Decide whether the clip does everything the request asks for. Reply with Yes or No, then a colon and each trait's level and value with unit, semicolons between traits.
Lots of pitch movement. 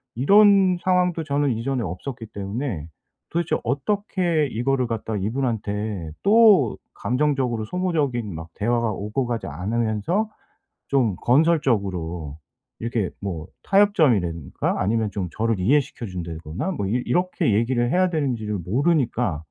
Yes: wide, 6.9 semitones